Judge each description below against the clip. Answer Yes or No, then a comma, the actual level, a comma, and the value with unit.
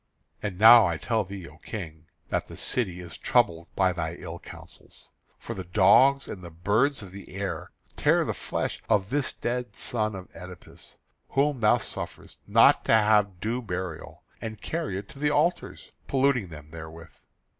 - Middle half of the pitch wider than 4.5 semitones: Yes, average, 5.3 semitones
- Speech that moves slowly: No, average, 175 wpm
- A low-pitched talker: Yes, low, 100 Hz